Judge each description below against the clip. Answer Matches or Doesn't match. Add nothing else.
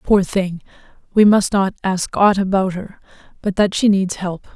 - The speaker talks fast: Doesn't match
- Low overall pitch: Doesn't match